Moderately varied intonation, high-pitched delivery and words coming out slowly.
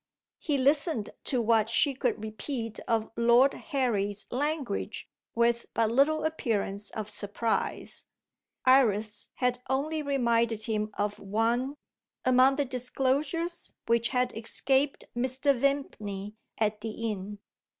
Yes: average, 4.0 semitones; high, 235 Hz; slow, 120 wpm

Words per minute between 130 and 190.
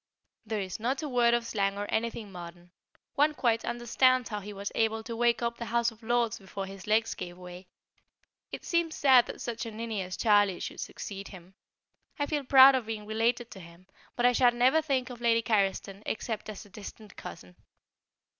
No: average, 200 wpm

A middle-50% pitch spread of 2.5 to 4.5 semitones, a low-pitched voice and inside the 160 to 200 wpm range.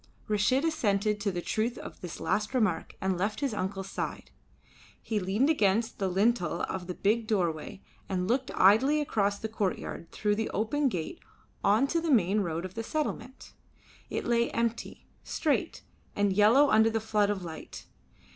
No: average, 3.5 semitones; high, 210 Hz; average, 170 wpm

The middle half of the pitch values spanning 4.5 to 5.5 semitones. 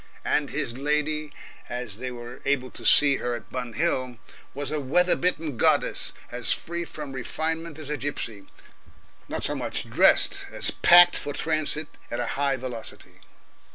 No: average, 3.8 semitones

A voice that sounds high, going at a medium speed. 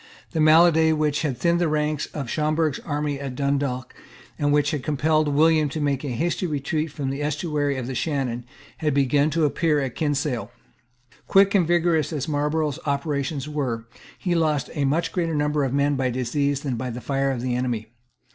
No: medium, 145 Hz; average, 190 wpm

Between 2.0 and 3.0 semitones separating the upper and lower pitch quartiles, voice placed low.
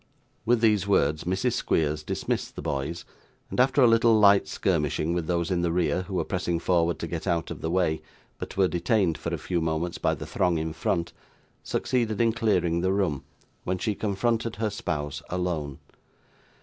No: average, 4.1 semitones; very low, 90 Hz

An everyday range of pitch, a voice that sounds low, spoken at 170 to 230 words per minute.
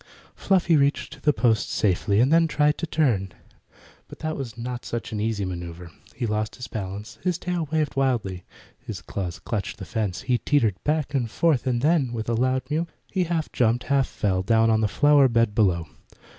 No: wide, 5.9 semitones; low, 120 Hz; average, 195 wpm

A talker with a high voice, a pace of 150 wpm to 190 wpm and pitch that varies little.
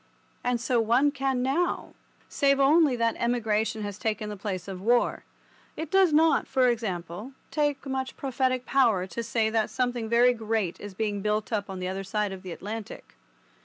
No: high, 230 Hz; average, 180 wpm; average, 4.1 semitones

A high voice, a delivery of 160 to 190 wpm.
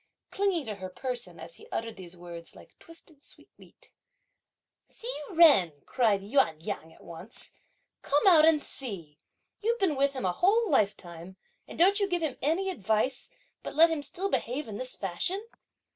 Yes: very high, 265 Hz; average, 170 wpm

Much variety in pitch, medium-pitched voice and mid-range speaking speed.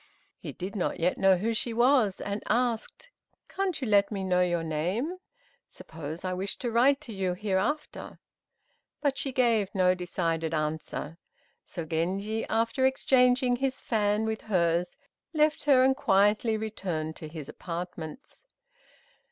No: wide, 5.8 semitones; high, 205 Hz; average, 145 wpm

